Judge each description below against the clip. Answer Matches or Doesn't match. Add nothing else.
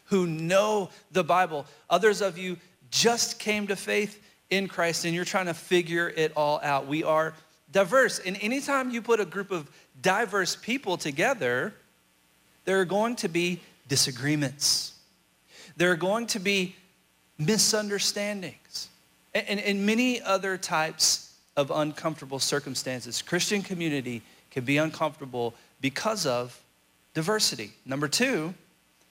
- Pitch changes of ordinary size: Doesn't match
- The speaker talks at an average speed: Doesn't match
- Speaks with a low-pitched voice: Doesn't match